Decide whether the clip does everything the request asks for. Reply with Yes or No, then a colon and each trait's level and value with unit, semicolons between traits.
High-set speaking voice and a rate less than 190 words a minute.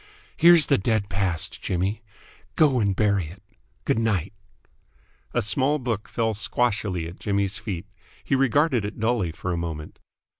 No: low, 105 Hz; average, 150 wpm